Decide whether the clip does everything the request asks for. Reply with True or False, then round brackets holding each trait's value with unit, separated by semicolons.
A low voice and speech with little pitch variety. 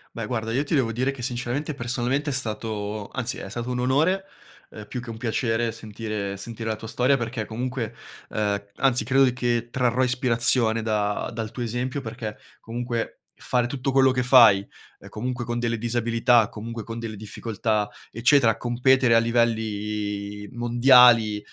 True (120 Hz; 2.3 semitones)